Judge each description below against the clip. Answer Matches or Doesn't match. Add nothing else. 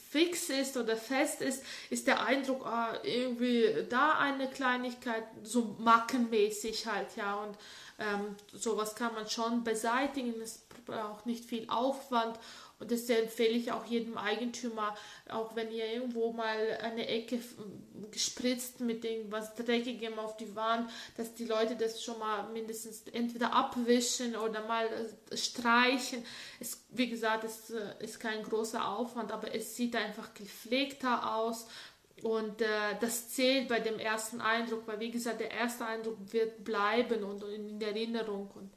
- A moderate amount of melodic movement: Doesn't match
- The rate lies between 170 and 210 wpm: Doesn't match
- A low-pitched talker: Doesn't match